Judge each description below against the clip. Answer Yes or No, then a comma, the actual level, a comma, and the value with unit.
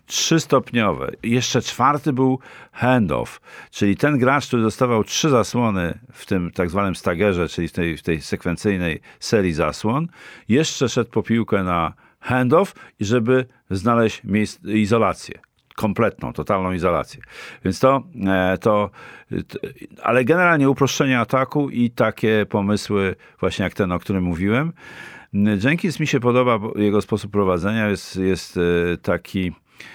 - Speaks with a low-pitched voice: Yes, low, 105 Hz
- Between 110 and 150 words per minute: Yes, average, 130 wpm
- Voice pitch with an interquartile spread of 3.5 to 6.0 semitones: Yes, average, 5.1 semitones